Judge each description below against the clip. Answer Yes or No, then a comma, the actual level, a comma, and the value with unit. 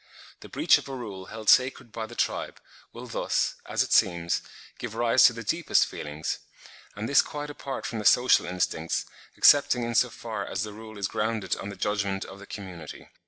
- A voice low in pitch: Yes, low, 110 Hz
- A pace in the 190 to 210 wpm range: Yes, average, 195 wpm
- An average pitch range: Yes, average, 3.7 semitones